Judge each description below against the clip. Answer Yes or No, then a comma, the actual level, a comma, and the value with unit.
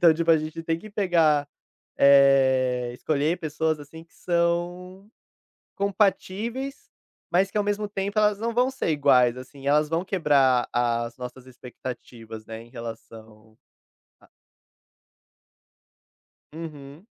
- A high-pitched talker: No, medium, 155 Hz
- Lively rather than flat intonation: Yes, wide, 6.3 semitones